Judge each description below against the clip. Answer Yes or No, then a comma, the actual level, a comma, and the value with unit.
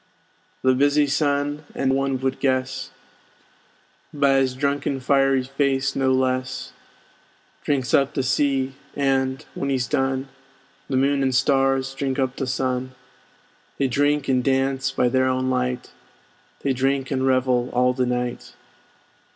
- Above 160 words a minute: No, average, 140 wpm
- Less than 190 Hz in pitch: Yes, low, 135 Hz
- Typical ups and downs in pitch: No, narrow, 1.0 semitones